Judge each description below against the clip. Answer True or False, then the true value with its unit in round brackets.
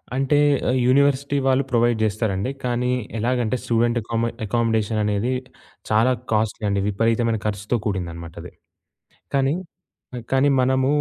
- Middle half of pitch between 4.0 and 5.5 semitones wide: False (3.2 semitones)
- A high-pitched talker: False (115 Hz)